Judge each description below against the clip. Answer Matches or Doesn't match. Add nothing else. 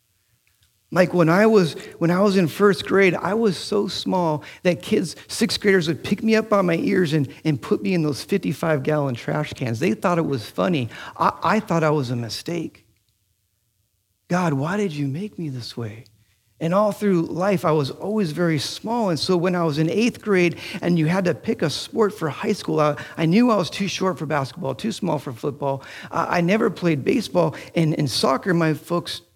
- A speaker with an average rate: Doesn't match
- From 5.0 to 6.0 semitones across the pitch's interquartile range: Matches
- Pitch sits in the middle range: Matches